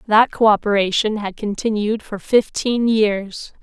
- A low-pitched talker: No, high, 215 Hz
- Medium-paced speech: No, slow, 115 wpm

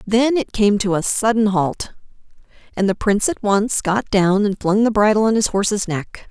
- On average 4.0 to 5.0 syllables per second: Yes, 4.9 syllables/s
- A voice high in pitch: Yes, high, 210 Hz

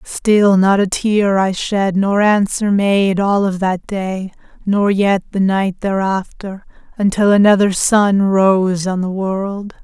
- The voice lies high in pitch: Yes, high, 195 Hz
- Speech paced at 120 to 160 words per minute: Yes, average, 155 wpm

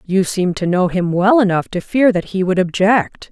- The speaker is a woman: Yes, female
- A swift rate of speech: Yes, fast, 235 wpm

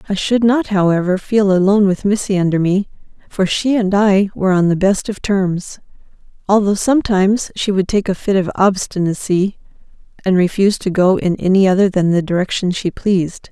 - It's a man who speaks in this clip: No, female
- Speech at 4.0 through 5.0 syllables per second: No, 5.4 syllables/s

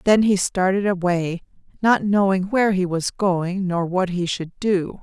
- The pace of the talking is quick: No, average, 180 wpm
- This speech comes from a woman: Yes, female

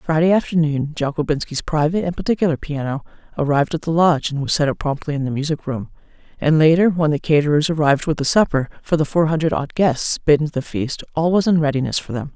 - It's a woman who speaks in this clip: Yes, female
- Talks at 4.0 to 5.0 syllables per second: No, 6.4 syllables/s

